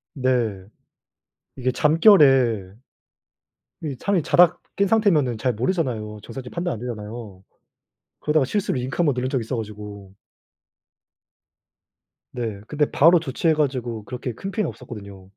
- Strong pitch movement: Yes, wide, 5.9 semitones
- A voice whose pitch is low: Yes, low, 125 Hz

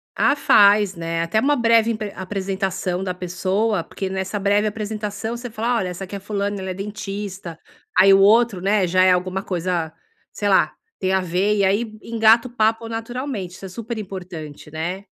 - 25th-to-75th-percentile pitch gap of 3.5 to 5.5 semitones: No, average, 2.8 semitones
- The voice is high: Yes, high, 200 Hz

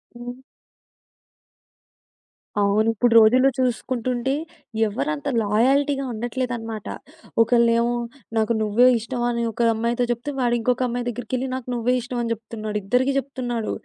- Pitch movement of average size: No, narrow, 1.9 semitones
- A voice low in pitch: No, high, 240 Hz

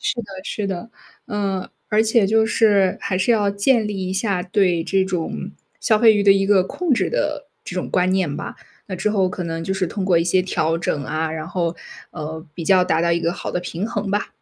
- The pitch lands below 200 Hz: Yes, high, 190 Hz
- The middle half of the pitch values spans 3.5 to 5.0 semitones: No, average, 3.1 semitones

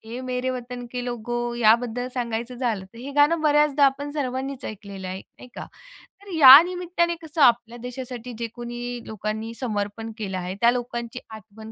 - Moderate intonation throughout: Yes, average, 3.2 semitones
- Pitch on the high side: Yes, high, 245 Hz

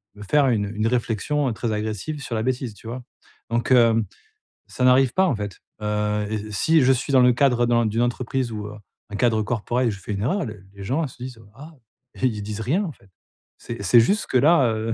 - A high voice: No, low, 120 Hz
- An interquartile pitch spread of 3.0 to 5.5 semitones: Yes, average, 3.4 semitones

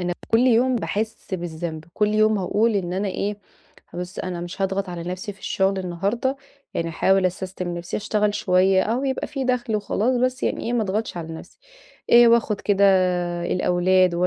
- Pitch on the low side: No, high, 195 Hz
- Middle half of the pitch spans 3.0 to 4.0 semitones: Yes, average, 3.7 semitones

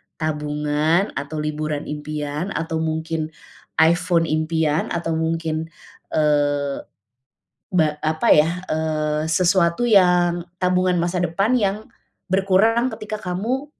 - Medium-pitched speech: Yes, medium, 160 Hz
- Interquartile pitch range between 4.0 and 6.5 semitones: No, average, 3.0 semitones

